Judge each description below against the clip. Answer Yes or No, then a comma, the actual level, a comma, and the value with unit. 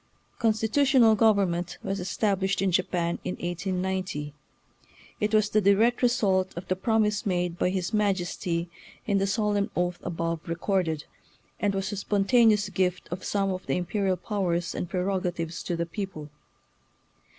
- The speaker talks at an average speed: Yes, average, 155 wpm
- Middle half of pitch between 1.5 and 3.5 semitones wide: Yes, average, 2.9 semitones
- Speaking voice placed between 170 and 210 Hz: Yes, high, 190 Hz